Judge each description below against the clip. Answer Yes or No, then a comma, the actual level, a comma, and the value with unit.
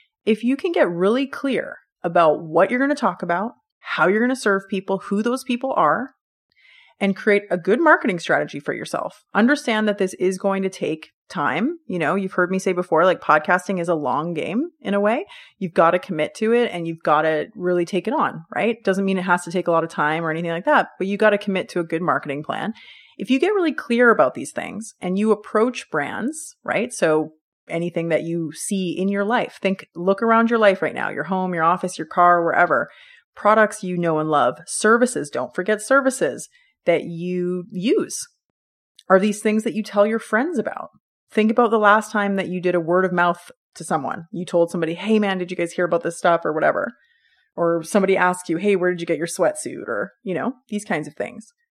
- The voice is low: No, high, 195 Hz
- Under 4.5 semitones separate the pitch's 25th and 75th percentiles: No, average, 4.8 semitones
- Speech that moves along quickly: Yes, fast, 225 wpm